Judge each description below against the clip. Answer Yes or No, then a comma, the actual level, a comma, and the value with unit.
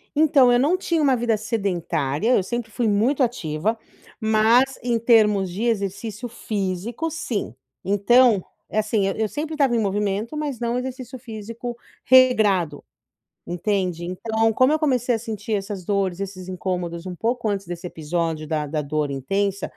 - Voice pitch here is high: Yes, high, 215 Hz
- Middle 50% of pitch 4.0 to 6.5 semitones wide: Yes, average, 4.6 semitones